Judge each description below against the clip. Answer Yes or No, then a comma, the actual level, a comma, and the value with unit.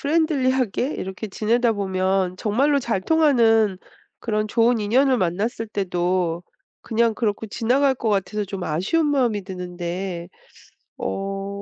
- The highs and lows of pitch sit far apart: No, average, 4.6 semitones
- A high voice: Yes, high, 215 Hz